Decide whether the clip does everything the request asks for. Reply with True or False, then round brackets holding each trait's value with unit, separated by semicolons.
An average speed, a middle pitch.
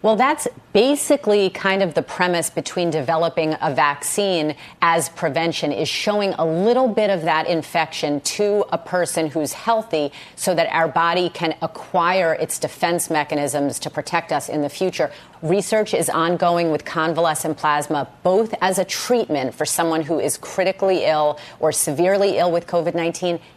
True (160 wpm; 165 Hz)